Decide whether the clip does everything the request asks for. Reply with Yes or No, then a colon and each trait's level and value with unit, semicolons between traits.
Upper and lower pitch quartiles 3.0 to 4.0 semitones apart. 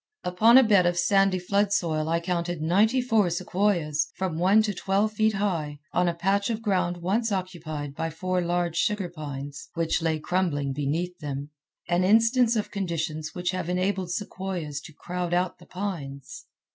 Yes: average, 3.7 semitones